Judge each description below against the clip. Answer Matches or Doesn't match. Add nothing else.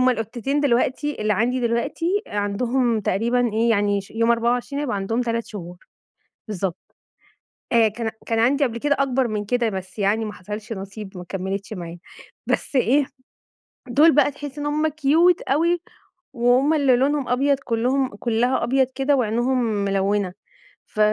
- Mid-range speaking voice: Doesn't match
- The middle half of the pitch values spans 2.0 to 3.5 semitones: Doesn't match